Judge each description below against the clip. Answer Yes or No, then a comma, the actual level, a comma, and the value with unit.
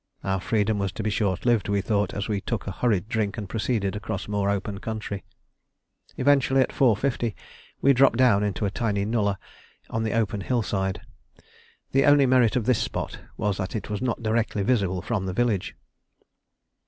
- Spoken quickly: No, average, 180 wpm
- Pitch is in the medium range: No, low, 105 Hz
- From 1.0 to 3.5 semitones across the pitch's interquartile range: Yes, average, 3.0 semitones